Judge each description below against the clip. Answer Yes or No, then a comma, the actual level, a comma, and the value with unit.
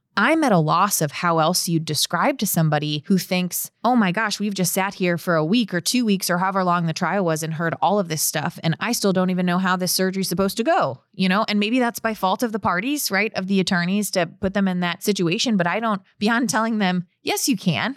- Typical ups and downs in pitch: Yes, average, 3.7 semitones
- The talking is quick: Yes, fast, 265 wpm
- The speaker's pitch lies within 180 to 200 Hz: Yes, high, 190 Hz